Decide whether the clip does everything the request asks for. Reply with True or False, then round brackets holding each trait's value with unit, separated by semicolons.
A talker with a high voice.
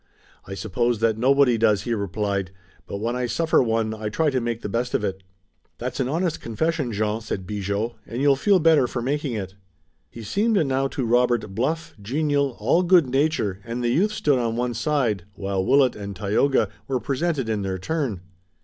False (120 Hz)